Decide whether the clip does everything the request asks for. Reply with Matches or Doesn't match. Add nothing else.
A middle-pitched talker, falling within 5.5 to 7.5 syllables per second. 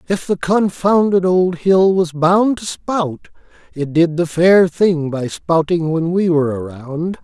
Doesn't match